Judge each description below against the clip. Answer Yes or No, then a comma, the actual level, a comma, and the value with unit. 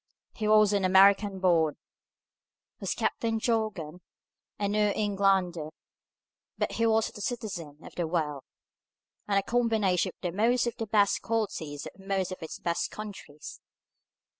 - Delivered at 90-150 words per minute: Yes, average, 140 wpm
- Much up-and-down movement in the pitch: No, average, 3.4 semitones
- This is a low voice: No, high, 200 Hz